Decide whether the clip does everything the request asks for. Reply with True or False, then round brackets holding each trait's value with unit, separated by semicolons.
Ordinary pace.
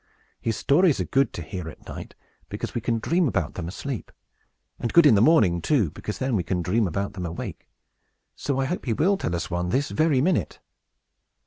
False (210 wpm)